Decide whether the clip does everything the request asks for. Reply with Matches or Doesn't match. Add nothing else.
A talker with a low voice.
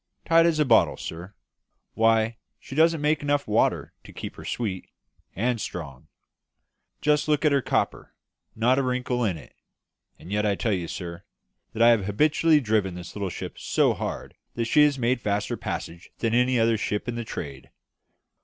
Matches